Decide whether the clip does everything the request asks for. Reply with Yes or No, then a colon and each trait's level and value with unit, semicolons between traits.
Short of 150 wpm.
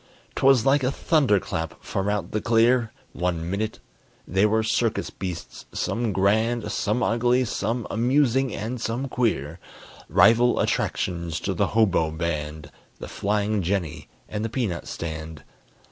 Yes: average, 140 wpm